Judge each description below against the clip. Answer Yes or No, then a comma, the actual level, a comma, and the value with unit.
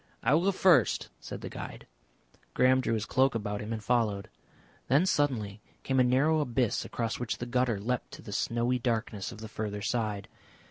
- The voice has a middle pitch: No, low, 120 Hz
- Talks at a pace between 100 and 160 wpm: No, average, 190 wpm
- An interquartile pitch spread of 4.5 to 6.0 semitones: No, average, 3.3 semitones